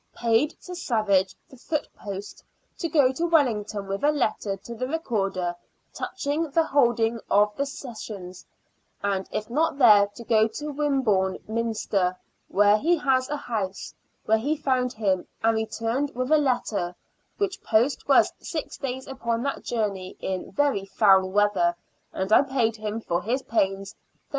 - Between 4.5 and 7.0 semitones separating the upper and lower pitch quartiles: Yes, wide, 5.4 semitones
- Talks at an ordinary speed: Yes, average, 160 wpm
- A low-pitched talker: No, high, 230 Hz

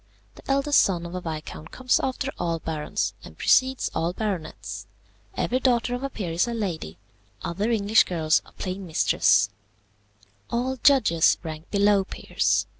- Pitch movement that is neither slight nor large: No, wide, 6.9 semitones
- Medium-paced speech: Yes, average, 155 wpm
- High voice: Yes, high, 195 Hz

